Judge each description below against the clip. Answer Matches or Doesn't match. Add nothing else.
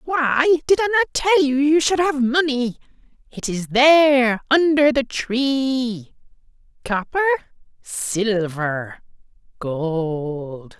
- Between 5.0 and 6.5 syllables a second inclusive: Doesn't match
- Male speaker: Matches